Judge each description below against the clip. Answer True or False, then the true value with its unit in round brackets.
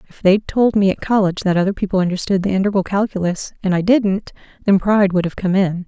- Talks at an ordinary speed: False (225 wpm)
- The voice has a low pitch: False (190 Hz)